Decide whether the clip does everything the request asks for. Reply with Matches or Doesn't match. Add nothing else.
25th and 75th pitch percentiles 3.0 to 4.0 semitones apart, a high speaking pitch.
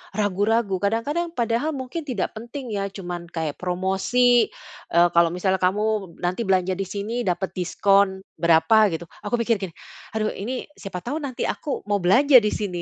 Doesn't match